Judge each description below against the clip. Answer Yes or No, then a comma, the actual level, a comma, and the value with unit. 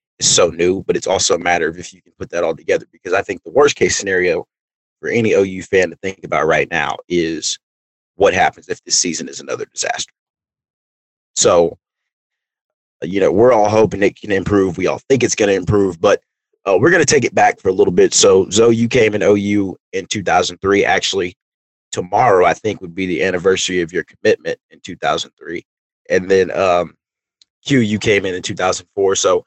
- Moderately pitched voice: No, low, 110 Hz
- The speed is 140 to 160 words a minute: No, fast, 205 wpm